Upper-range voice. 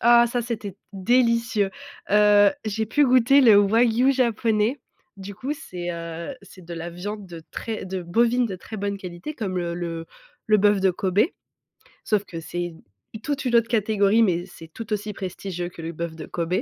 Yes: high, 205 Hz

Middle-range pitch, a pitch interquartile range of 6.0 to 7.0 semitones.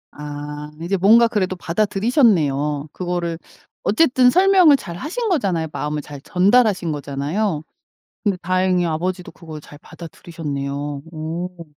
No: medium, 175 Hz; wide, 5.6 semitones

